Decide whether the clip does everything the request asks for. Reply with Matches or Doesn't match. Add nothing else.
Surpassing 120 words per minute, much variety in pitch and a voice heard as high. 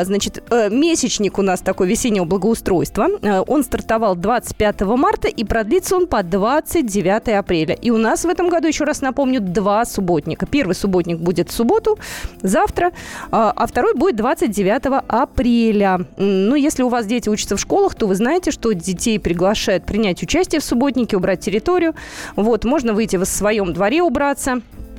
Matches